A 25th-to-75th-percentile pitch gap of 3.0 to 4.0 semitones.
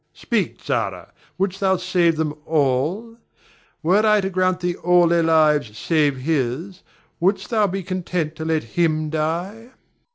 Yes: average, 3.3 semitones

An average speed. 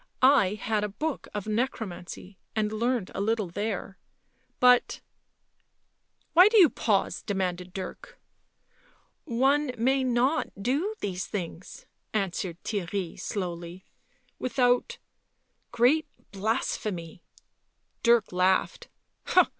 No: slow, 115 wpm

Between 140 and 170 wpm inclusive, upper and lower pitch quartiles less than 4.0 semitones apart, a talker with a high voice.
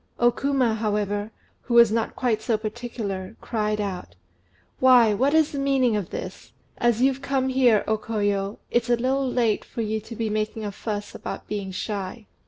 No: average, 185 wpm; average, 3.0 semitones; high, 225 Hz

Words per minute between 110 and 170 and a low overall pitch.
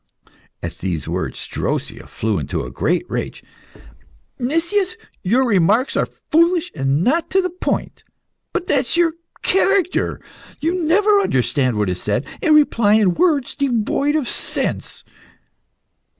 No: slow, 135 wpm; very high, 280 Hz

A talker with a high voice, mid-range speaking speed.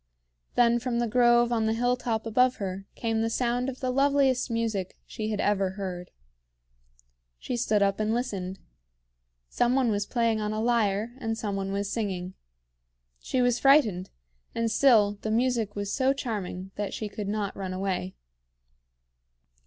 Yes: high, 220 Hz; average, 160 wpm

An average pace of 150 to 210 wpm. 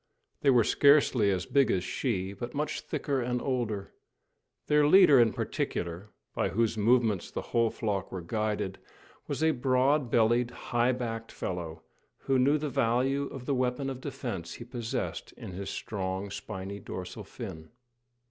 Yes: average, 155 wpm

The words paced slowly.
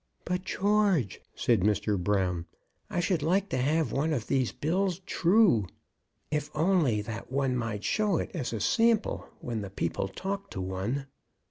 No: average, 160 wpm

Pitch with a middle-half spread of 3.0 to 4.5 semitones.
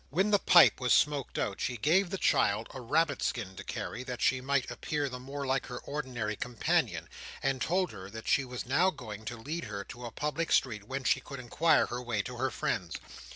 Yes: average, 3.6 semitones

